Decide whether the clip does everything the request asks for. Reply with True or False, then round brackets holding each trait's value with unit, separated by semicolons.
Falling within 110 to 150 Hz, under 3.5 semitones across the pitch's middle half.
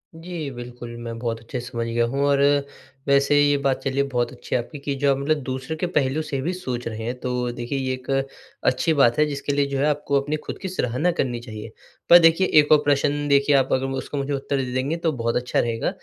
True (135 Hz; 3.0 semitones)